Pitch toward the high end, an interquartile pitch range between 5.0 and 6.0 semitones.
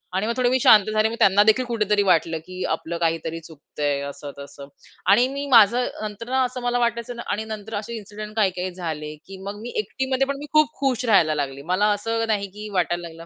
Yes: high, 210 Hz; wide, 5.5 semitones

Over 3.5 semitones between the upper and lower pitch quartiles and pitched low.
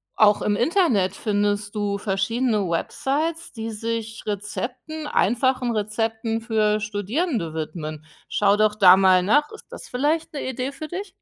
No: average, 4.2 semitones; high, 220 Hz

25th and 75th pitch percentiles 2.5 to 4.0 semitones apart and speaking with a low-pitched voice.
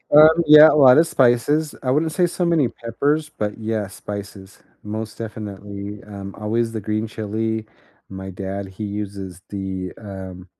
No: average, 4.5 semitones; low, 110 Hz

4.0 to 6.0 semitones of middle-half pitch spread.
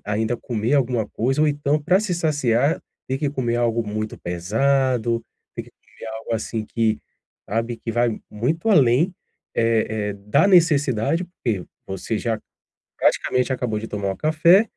Yes: average, 4.9 semitones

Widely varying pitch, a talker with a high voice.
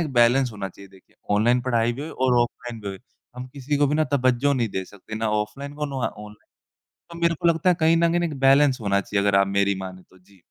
No: wide, 5.9 semitones; low, 125 Hz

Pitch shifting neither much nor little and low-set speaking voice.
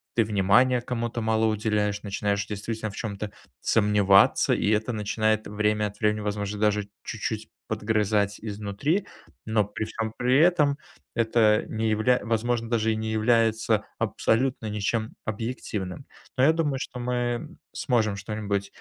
No: narrow, 2.2 semitones; low, 110 Hz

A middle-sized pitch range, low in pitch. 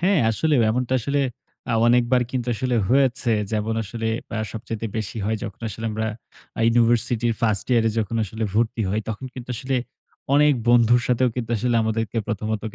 No: narrow, 2.1 semitones; low, 115 Hz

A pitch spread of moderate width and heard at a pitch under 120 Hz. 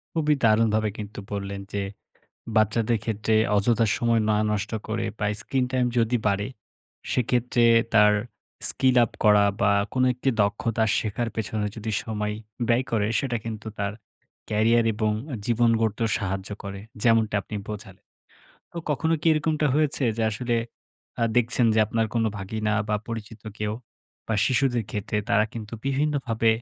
No: narrow, 2.2 semitones; low, 110 Hz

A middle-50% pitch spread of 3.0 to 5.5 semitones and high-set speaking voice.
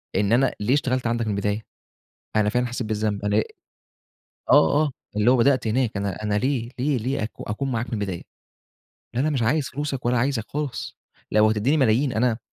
No: average, 3.7 semitones; low, 120 Hz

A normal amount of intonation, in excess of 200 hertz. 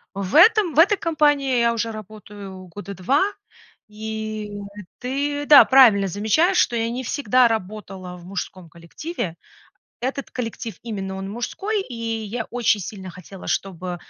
No: wide, 5.7 semitones; high, 220 Hz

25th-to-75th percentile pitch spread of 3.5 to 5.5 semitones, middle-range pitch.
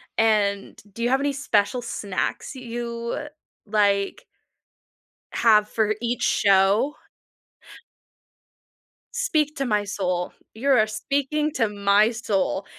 No: average, 4.3 semitones; high, 220 Hz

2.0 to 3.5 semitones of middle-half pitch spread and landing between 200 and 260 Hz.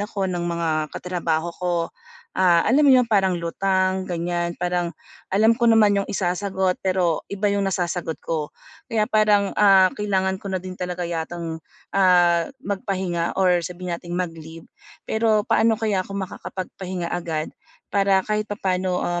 No: narrow, 2.4 semitones; medium, 185 Hz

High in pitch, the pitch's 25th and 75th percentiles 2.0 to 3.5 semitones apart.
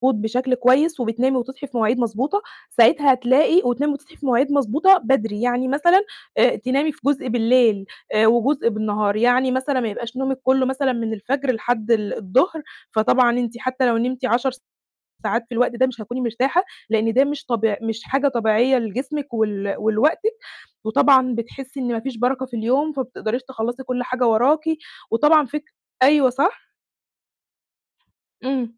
Yes: very high, 250 Hz; average, 2.9 semitones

